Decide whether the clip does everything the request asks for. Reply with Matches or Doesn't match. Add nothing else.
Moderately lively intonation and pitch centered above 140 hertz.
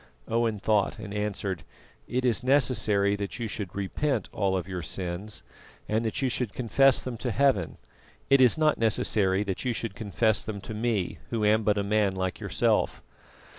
Doesn't match